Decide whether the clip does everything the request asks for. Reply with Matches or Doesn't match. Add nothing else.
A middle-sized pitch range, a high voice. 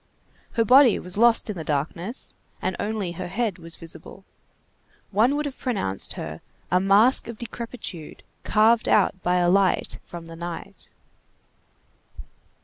Matches